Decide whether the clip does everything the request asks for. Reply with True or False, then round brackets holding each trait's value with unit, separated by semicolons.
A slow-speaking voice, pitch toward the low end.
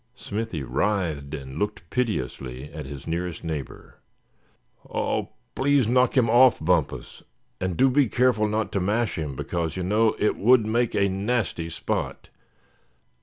False (145 wpm; 100 Hz)